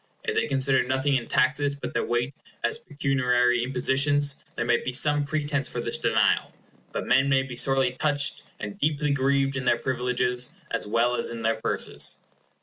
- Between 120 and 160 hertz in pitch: Yes, low, 135 Hz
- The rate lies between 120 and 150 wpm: No, average, 180 wpm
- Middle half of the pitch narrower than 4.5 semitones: Yes, narrow, 2.5 semitones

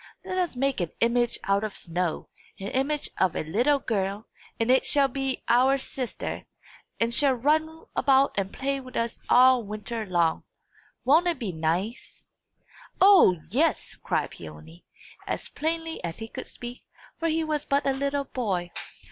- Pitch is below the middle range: No, very high, 250 Hz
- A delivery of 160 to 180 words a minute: Yes, average, 165 wpm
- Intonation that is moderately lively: No, wide, 6.1 semitones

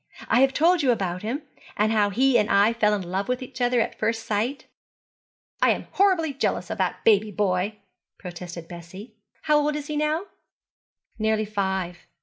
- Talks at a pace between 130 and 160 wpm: No, average, 180 wpm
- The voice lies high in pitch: Yes, high, 220 Hz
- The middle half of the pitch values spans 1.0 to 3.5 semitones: No, average, 5.3 semitones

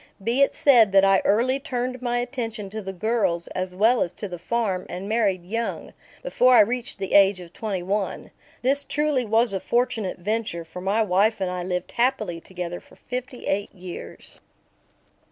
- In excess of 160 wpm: Yes, average, 185 wpm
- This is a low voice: No, high, 210 Hz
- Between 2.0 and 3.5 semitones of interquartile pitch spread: No, average, 4.6 semitones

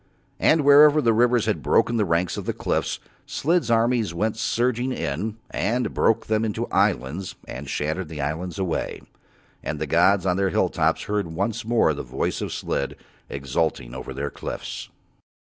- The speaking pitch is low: Yes, low, 100 Hz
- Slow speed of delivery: No, average, 175 wpm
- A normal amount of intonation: No, wide, 6.8 semitones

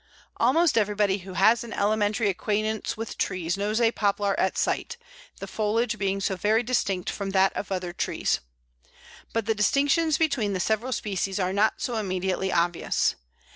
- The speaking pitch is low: No, high, 205 Hz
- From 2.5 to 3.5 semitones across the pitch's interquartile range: Yes, average, 2.8 semitones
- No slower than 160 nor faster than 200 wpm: Yes, average, 165 wpm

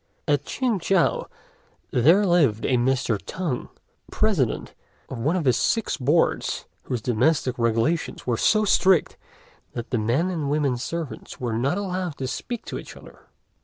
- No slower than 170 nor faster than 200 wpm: No, average, 155 wpm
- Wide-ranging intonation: Yes, wide, 6.4 semitones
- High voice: No, medium, 145 Hz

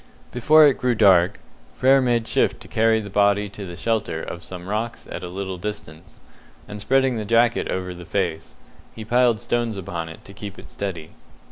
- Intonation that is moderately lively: Yes, average, 3.9 semitones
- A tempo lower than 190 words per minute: No, average, 195 wpm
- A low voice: Yes, low, 105 Hz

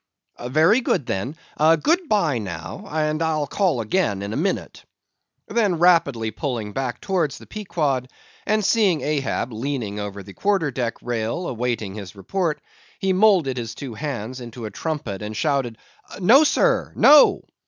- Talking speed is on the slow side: No, average, 150 wpm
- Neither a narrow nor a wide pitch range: No, wide, 7.9 semitones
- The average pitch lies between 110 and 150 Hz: Yes, medium, 140 Hz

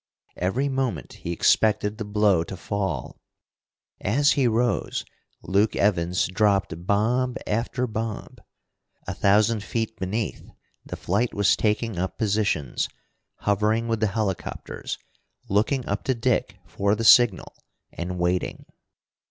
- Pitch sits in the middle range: No, low, 105 Hz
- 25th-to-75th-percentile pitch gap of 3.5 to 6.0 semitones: No, average, 2.9 semitones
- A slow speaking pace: Yes, slow, 125 wpm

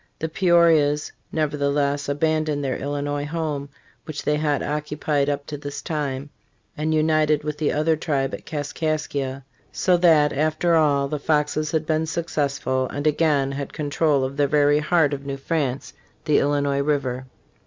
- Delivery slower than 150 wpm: No, average, 160 wpm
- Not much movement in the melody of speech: Yes, narrow, 1.6 semitones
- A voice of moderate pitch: Yes, medium, 150 Hz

